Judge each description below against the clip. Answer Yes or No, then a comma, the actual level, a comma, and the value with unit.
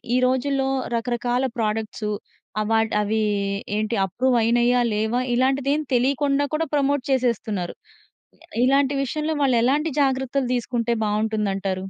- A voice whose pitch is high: Yes, high, 245 Hz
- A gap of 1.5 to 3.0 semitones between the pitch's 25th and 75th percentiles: No, average, 3.6 semitones